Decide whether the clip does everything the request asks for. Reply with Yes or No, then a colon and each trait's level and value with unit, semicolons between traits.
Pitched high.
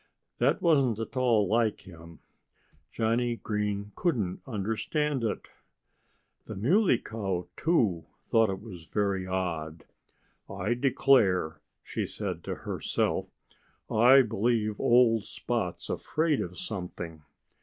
No: low, 110 Hz